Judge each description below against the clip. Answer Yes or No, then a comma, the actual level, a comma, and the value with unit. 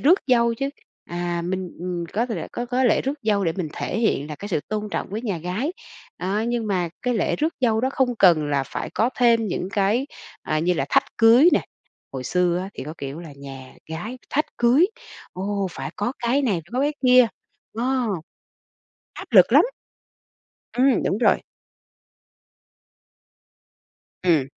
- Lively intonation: Yes, wide, 5.9 semitones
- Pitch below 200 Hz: No, high, 210 Hz